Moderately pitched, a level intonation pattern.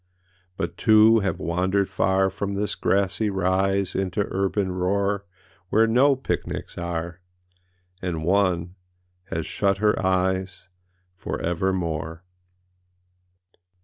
No: very low, 95 Hz; narrow, 1.8 semitones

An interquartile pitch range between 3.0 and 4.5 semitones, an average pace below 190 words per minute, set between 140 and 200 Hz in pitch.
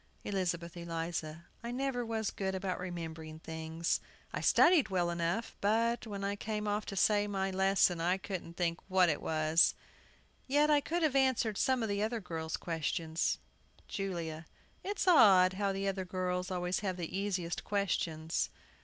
Yes: average, 3.7 semitones; average, 160 wpm; high, 190 Hz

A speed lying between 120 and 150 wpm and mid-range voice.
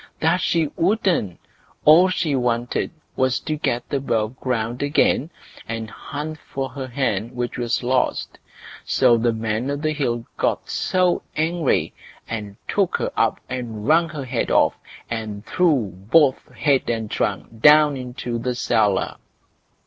No: average, 140 wpm; low, 125 Hz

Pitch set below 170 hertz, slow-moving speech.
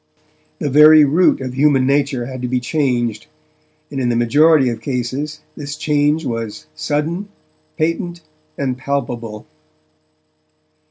Yes: medium, 140 Hz; slow, 125 wpm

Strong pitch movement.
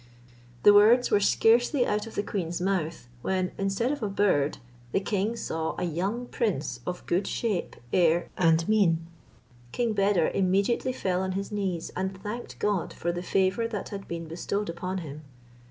No: average, 3.3 semitones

